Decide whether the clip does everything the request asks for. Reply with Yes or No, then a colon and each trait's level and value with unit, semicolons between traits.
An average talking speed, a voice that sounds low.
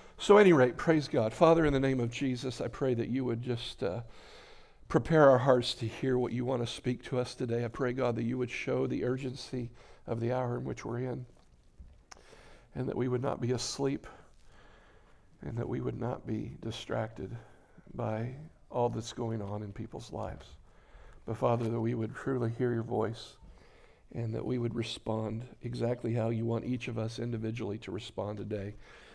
Yes: average, 195 wpm; low, 120 Hz